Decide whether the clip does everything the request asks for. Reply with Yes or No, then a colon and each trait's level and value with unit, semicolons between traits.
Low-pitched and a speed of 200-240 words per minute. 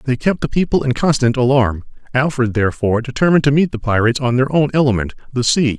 Yes: low, 130 Hz; fast, 205 wpm